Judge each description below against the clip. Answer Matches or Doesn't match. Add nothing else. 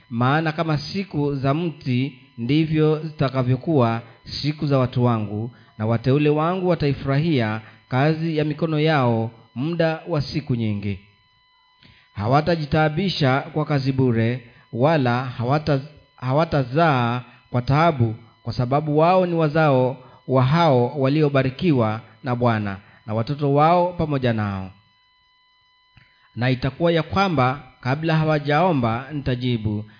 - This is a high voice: Doesn't match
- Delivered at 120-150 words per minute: Doesn't match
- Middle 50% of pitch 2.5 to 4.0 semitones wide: Doesn't match